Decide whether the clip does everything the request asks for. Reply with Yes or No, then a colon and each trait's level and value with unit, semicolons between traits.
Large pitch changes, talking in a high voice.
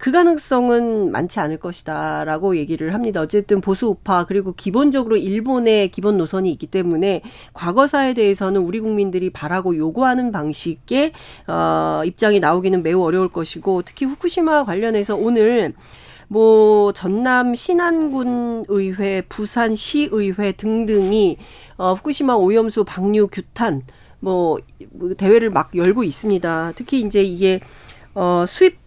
No: average, 4.1 semitones; high, 205 Hz